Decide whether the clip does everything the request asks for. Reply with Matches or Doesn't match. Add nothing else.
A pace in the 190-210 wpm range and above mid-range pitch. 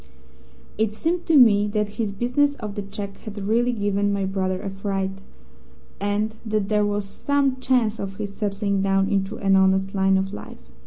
Doesn't match